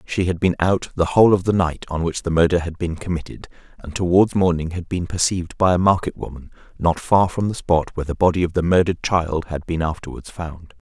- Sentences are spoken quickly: Yes, fast, 230 wpm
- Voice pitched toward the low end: Yes, very low, 85 Hz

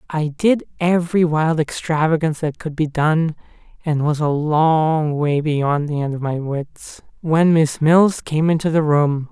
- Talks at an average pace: Yes, average, 175 wpm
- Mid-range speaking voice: Yes, medium, 155 Hz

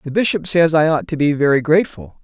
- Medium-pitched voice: Yes, medium, 155 Hz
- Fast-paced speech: Yes, fast, 240 wpm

